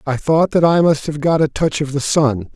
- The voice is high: No, medium, 150 Hz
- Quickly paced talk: Yes, fast, 280 wpm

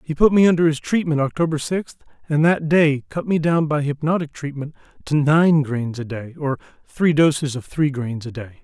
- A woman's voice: No, male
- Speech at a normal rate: No, fast, 210 wpm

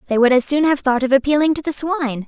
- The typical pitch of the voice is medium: No, very high, 275 Hz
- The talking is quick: Yes, fast, 290 wpm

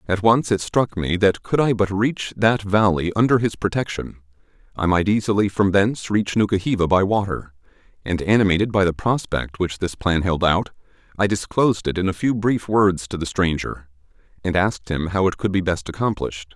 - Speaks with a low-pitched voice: Yes, very low, 95 Hz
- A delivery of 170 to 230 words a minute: Yes, average, 195 wpm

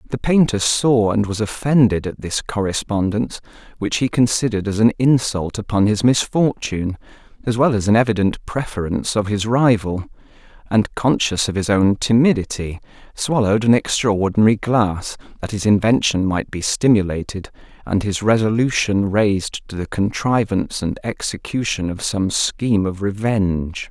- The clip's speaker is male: Yes, male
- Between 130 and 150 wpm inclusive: Yes, average, 145 wpm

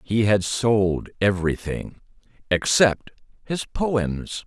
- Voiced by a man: Yes, male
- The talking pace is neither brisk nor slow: No, slow, 80 wpm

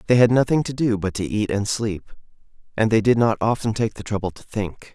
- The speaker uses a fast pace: Yes, fast, 245 wpm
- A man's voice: Yes, male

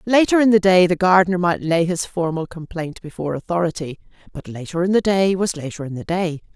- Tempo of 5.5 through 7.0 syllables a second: Yes, 5.9 syllables/s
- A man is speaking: No, female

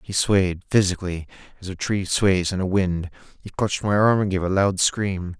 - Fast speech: Yes, fast, 210 wpm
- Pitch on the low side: Yes, very low, 95 Hz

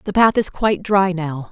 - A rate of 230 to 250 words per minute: Yes, fast, 235 wpm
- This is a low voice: No, medium, 185 Hz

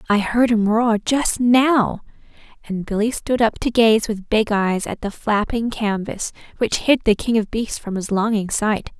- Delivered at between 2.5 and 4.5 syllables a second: Yes, 4.2 syllables/s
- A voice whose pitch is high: Yes, high, 220 Hz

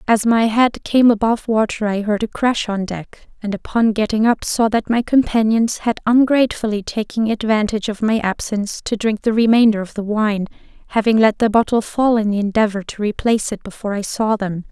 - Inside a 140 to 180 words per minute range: No, average, 200 wpm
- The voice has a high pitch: Yes, high, 220 Hz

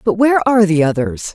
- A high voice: Yes, high, 195 Hz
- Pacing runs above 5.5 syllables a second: Yes, 6.4 syllables/s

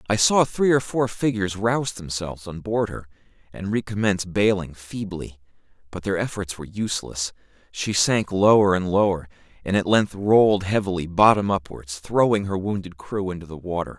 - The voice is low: Yes, low, 100 Hz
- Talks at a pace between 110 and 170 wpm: Yes, average, 165 wpm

